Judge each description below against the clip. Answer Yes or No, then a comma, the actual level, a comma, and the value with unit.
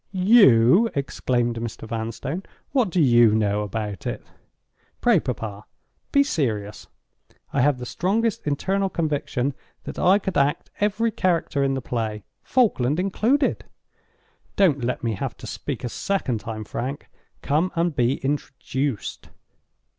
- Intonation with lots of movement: Yes, wide, 8.1 semitones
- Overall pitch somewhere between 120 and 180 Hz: Yes, medium, 140 Hz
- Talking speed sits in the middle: No, slow, 130 wpm